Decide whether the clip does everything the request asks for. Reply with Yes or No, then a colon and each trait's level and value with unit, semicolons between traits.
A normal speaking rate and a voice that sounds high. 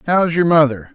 No: average, 190 wpm; medium, 150 Hz